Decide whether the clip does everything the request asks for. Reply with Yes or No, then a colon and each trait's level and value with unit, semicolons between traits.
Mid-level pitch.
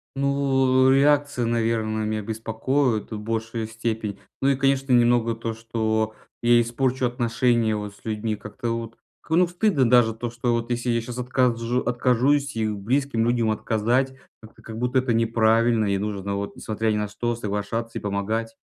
No: low, 115 Hz